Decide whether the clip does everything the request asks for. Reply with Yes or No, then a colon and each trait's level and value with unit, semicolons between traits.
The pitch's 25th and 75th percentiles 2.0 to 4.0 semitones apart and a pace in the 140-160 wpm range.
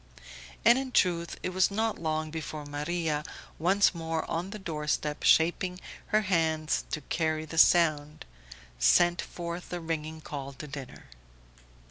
Yes: narrow, 2.5 semitones; average, 145 wpm